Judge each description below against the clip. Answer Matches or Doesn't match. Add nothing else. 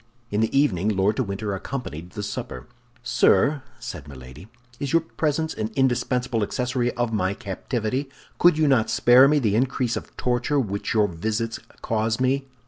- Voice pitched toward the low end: Matches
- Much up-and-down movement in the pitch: Doesn't match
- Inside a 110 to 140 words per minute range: Doesn't match